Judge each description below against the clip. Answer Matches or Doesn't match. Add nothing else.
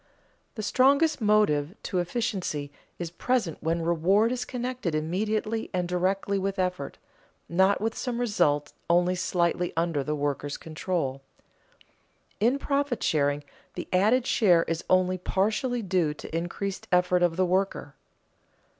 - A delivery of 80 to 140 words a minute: Matches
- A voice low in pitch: Doesn't match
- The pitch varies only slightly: Doesn't match